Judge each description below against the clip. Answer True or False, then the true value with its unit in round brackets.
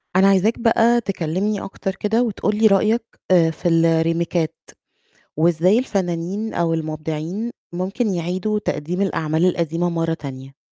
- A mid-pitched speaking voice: True (180 Hz)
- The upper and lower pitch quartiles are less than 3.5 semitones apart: False (4.2 semitones)